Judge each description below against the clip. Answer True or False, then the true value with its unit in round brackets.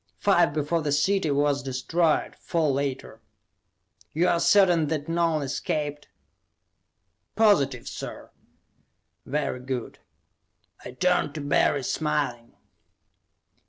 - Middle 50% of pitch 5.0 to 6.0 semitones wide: False (3.4 semitones)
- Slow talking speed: True (100 wpm)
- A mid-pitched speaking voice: True (150 Hz)